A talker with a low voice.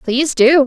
No: very high, 270 Hz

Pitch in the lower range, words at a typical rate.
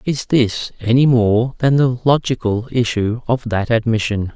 Yes: low, 120 Hz; average, 150 wpm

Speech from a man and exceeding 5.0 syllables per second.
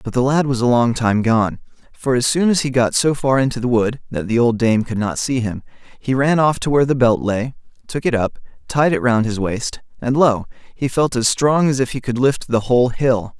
Yes: male; 5.2 syllables/s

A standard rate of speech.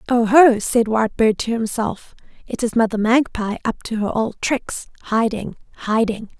Yes: average, 150 wpm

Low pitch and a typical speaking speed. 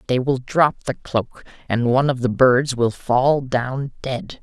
Yes: low, 130 Hz; average, 190 wpm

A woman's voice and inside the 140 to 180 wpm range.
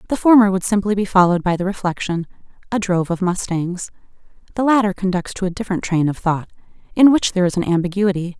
No: female; average, 200 wpm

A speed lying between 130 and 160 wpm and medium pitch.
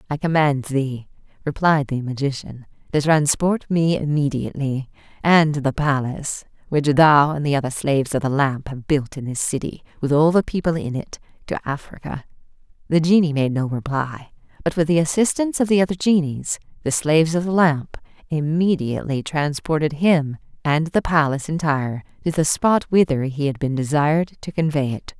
No: average, 170 wpm; medium, 150 Hz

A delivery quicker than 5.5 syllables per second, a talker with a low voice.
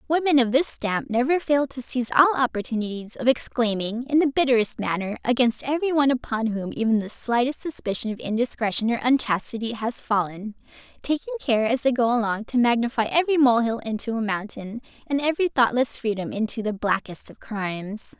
No: 5.7 syllables/s; high, 240 Hz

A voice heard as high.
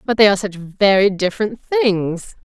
Yes: high, 205 Hz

